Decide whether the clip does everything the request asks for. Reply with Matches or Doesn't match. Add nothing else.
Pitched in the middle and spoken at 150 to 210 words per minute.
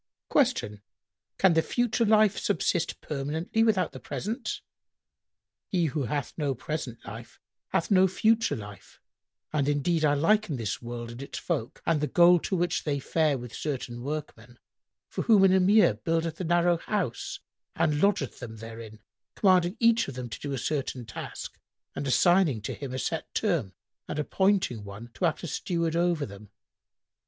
Matches